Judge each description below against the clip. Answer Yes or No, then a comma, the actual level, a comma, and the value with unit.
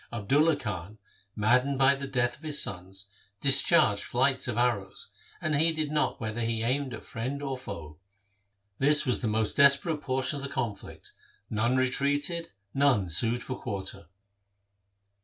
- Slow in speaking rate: No, average, 155 wpm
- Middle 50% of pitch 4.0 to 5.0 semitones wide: Yes, average, 4.4 semitones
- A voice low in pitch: Yes, low, 130 Hz